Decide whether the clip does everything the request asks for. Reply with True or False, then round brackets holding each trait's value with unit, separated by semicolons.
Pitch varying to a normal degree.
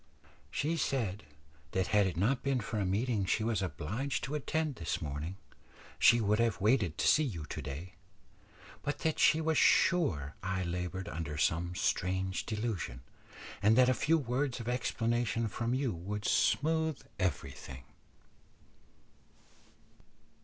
False (6.2 semitones)